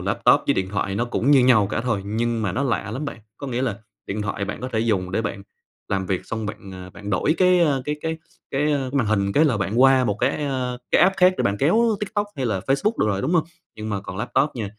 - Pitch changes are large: Yes, wide, 5.7 semitones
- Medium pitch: No, low, 115 Hz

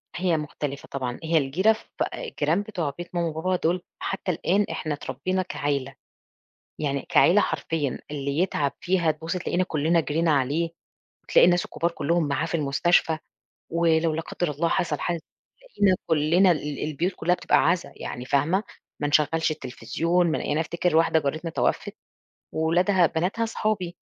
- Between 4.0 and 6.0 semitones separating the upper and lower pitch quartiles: No, average, 3.2 semitones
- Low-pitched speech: No, medium, 165 Hz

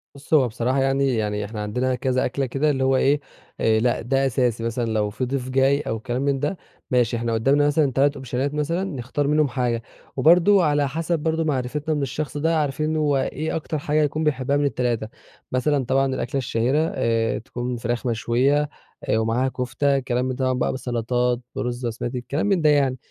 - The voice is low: Yes, low, 130 Hz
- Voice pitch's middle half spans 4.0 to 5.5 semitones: No, average, 3.2 semitones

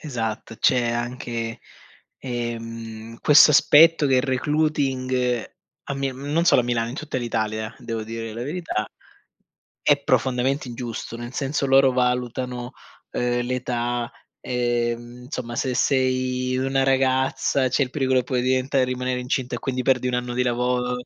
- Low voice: Yes, low, 125 Hz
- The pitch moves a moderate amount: No, narrow, 1.8 semitones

